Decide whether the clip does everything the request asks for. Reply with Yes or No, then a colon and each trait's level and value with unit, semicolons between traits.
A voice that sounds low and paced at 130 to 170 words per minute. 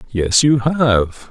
Yes: low, 120 Hz; average, 140 wpm